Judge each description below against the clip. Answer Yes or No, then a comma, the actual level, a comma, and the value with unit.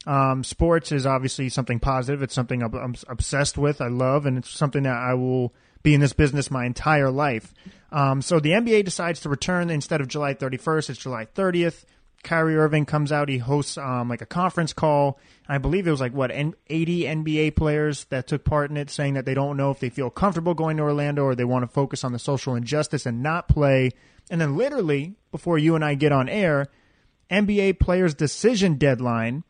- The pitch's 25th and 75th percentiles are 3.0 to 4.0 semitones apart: Yes, average, 3.3 semitones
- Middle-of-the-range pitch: Yes, medium, 145 Hz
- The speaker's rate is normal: No, fast, 210 wpm